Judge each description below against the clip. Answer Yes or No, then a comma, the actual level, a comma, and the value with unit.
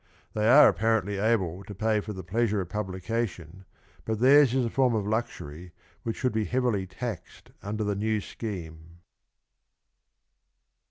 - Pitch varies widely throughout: No, average, 3.4 semitones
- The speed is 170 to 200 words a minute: No, average, 155 wpm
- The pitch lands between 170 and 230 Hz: No, low, 105 Hz